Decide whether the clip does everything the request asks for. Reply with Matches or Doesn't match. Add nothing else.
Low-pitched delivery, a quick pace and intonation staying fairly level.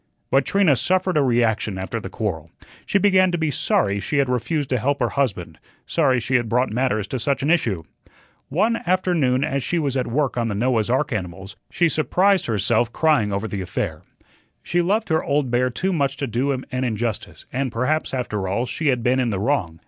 Doesn't match